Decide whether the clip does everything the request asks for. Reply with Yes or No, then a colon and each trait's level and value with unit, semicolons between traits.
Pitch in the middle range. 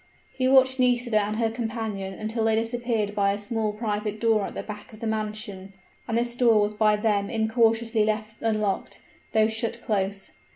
No: high, 220 Hz